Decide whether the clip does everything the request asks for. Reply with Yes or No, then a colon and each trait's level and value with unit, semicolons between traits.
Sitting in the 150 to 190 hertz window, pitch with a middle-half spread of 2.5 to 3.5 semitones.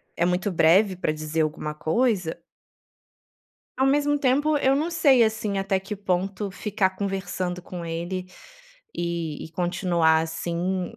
No: medium, 185 Hz; average, 4.0 semitones